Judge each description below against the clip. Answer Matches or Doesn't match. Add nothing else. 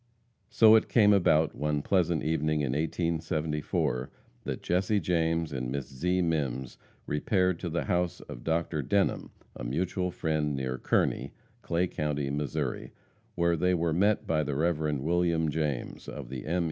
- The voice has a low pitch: Matches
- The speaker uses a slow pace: Doesn't match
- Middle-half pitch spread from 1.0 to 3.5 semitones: Matches